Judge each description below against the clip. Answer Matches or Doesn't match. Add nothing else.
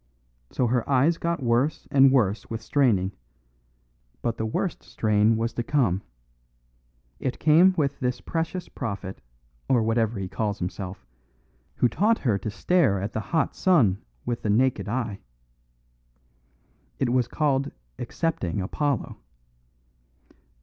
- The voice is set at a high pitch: Doesn't match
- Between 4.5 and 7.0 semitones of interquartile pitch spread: Matches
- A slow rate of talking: Matches